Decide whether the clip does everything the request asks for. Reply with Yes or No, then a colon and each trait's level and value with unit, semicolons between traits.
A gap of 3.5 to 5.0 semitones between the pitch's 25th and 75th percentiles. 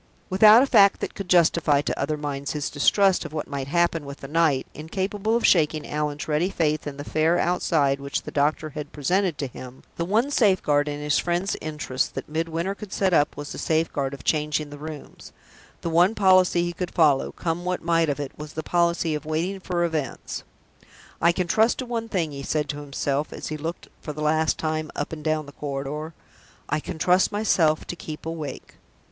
No: average, 3.1 semitones